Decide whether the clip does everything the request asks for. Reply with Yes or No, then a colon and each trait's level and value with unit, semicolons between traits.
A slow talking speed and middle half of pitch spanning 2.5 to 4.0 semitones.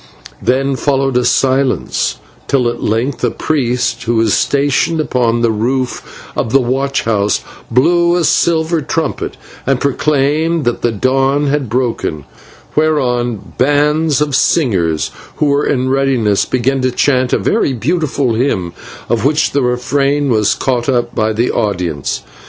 No: average, 145 wpm; average, 3.3 semitones